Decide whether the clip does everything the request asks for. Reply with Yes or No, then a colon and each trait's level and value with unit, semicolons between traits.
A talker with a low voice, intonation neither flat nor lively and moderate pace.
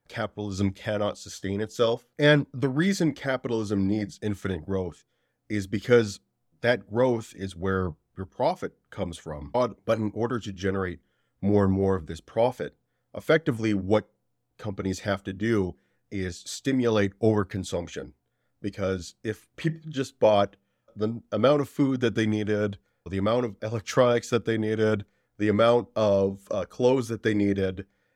Yes: low, 105 Hz; average, 3.2 semitones; average, 145 wpm